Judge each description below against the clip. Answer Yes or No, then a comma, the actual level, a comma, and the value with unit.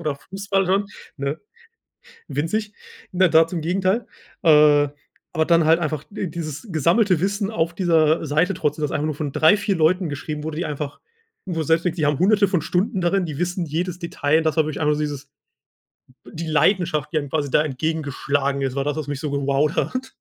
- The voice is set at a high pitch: No, medium, 160 Hz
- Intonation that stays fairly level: No, average, 3.3 semitones